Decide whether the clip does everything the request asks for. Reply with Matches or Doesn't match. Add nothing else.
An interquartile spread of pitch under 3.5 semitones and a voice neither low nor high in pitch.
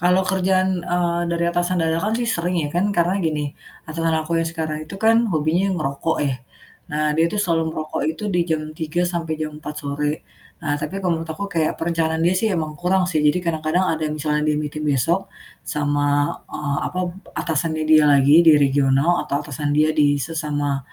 Matches